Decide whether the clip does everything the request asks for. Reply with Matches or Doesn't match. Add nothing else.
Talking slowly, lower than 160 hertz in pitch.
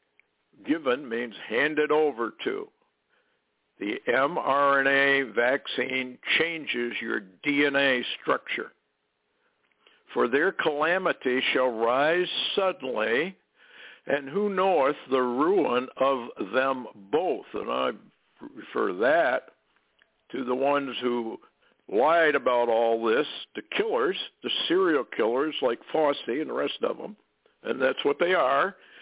Matches